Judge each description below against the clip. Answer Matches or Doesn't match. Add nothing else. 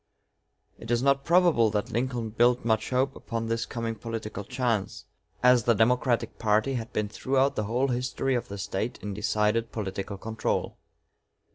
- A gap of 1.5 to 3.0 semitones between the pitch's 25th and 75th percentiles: Matches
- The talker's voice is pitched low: Matches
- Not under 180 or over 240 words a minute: Doesn't match